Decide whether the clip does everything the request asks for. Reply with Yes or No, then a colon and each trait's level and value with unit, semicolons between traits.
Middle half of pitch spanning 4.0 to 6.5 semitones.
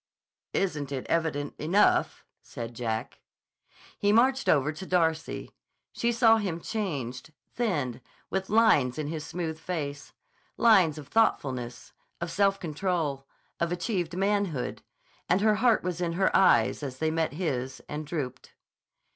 Yes: wide, 5.4 semitones